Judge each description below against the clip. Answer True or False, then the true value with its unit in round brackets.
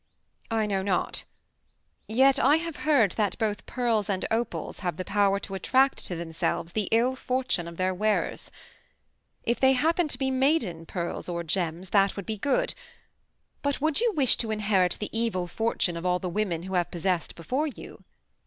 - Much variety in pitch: True (6.2 semitones)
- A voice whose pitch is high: True (210 Hz)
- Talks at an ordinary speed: True (180 wpm)